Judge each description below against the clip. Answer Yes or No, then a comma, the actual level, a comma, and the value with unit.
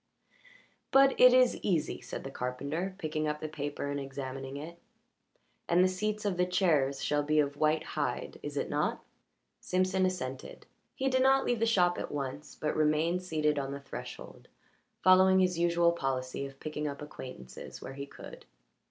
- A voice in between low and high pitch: Yes, medium, 155 Hz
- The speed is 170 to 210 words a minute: Yes, average, 175 wpm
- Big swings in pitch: No, average, 4.8 semitones